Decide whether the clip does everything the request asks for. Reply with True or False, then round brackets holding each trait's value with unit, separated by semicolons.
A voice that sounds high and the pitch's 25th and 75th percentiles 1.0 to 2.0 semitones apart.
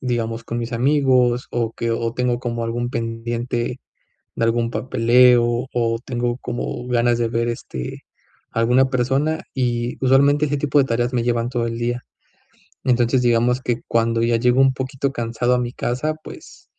False (120 Hz; 1.5 semitones)